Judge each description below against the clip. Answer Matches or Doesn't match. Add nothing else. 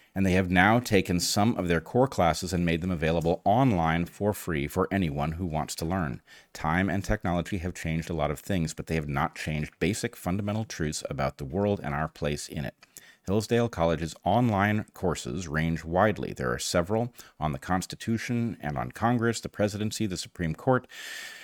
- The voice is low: Matches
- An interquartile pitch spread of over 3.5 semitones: Matches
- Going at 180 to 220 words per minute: Matches